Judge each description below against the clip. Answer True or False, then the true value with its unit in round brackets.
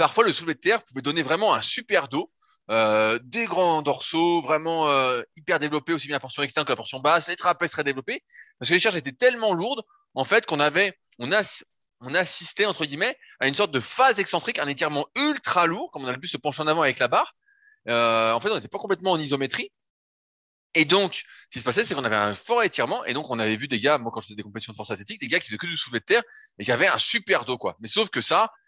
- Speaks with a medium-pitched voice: True (155 Hz)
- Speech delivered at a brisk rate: True (270 wpm)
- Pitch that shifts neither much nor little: False (6.6 semitones)